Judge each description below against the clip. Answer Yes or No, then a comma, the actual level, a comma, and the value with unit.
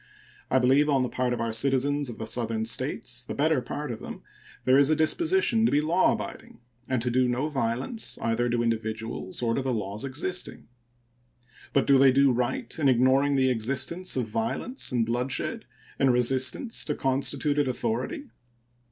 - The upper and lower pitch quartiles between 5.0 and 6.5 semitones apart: No, average, 3.2 semitones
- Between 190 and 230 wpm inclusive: No, average, 180 wpm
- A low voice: Yes, low, 130 Hz